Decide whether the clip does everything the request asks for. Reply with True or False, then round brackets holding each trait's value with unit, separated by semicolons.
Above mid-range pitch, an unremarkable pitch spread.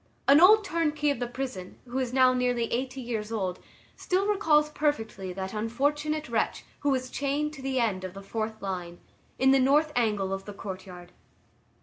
False (250 Hz; 6.1 semitones)